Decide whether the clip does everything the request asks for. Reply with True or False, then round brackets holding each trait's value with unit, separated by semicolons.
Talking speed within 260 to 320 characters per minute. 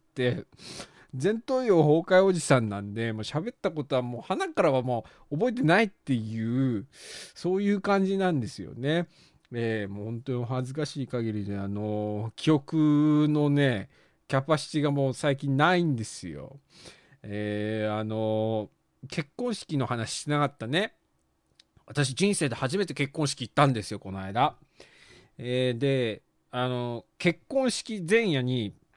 True (280 characters per minute)